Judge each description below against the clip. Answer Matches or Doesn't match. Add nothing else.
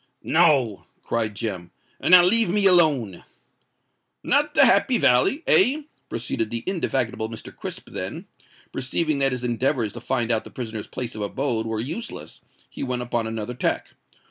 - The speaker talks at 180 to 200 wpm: Doesn't match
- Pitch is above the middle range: Doesn't match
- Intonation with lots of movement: Matches